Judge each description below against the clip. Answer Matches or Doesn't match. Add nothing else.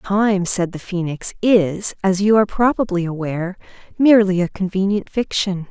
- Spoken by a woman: Matches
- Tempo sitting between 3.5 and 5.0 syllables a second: Matches